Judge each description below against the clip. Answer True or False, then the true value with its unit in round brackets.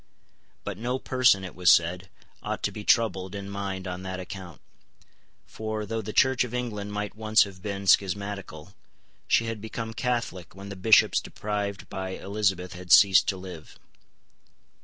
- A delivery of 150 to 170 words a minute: True (160 wpm)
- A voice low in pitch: True (100 Hz)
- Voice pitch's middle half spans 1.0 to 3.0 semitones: True (2.6 semitones)